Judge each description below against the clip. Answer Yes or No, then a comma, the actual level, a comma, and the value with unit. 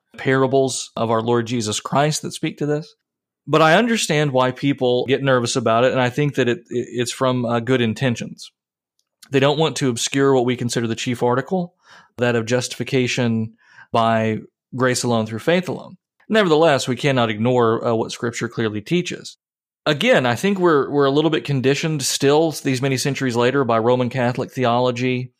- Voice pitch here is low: Yes, low, 130 Hz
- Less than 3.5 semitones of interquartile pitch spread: Yes, average, 3.0 semitones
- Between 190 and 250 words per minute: No, average, 180 wpm